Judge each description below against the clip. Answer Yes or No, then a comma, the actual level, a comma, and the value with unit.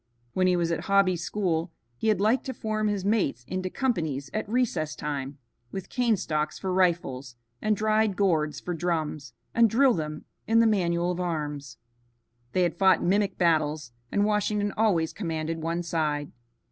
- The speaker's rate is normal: Yes, average, 170 wpm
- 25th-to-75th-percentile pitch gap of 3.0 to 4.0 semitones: No, average, 4.9 semitones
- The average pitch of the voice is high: No, medium, 180 Hz